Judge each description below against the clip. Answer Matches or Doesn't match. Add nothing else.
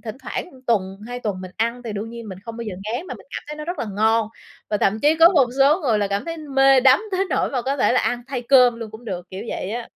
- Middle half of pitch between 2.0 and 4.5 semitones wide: Matches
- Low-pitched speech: Doesn't match